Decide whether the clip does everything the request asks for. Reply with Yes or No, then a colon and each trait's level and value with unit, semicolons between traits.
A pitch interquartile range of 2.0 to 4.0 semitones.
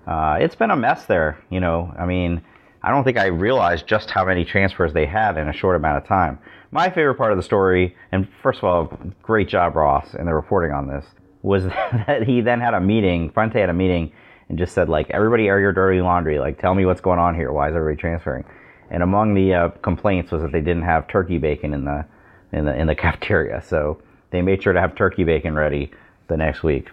Yes: average, 3.2 semitones